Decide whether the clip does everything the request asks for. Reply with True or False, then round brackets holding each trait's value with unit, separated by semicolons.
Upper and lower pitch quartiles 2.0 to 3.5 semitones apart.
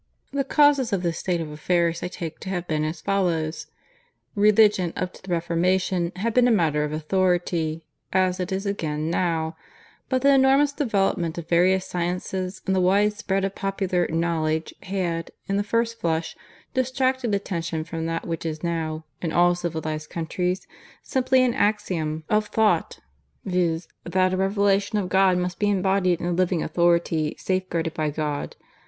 True (3.2 semitones)